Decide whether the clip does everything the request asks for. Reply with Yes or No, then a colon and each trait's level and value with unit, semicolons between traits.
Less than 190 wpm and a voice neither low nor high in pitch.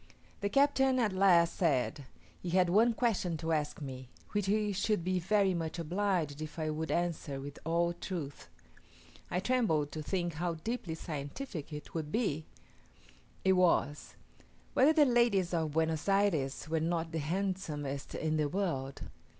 Yes: average, 160 wpm; medium, 170 Hz